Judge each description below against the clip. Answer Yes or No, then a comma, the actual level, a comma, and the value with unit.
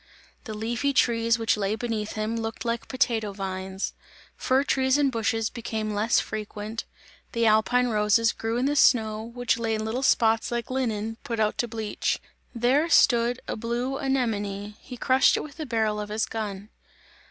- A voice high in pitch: Yes, high, 225 Hz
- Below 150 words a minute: No, average, 175 wpm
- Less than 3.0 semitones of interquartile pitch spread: Yes, narrow, 2.4 semitones